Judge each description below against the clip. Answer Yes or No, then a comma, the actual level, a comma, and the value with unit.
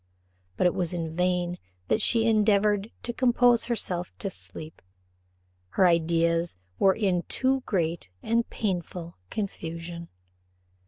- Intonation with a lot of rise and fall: No, average, 4.3 semitones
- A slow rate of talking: Yes, slow, 120 wpm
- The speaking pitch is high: No, medium, 180 Hz